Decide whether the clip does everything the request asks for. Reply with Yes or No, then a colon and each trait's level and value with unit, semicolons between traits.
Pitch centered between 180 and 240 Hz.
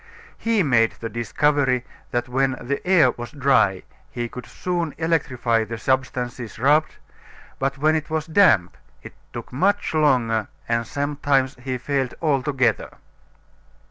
No: low, 135 Hz